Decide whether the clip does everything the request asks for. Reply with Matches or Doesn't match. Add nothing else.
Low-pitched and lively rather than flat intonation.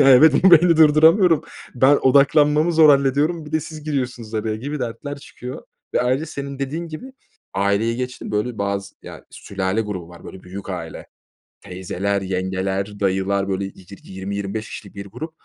Matches